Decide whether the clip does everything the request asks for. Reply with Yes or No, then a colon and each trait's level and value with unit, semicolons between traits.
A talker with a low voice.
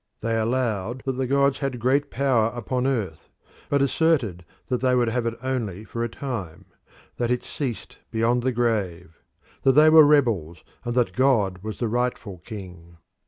Yes: low, 120 Hz